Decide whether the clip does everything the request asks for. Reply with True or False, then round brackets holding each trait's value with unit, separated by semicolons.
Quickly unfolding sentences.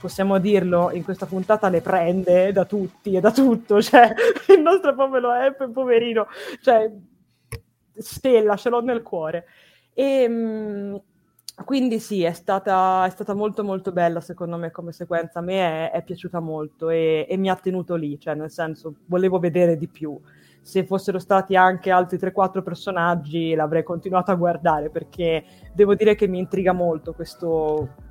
False (160 wpm)